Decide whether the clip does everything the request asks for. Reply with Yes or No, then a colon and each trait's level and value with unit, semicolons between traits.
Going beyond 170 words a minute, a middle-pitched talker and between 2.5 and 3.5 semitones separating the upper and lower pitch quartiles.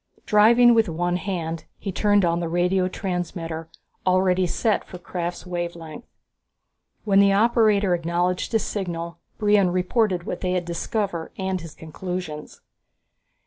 No: average, 140 wpm; medium, 180 Hz; average, 2.8 semitones